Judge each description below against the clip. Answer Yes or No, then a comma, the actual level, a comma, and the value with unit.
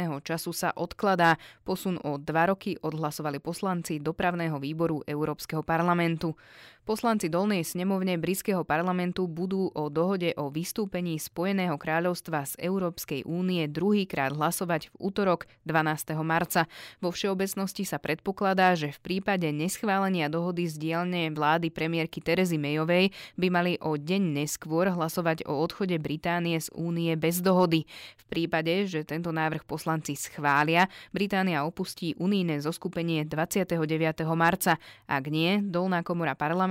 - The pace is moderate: Yes, average, 130 wpm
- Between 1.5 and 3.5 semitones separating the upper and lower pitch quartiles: Yes, narrow, 2.6 semitones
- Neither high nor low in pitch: Yes, medium, 170 Hz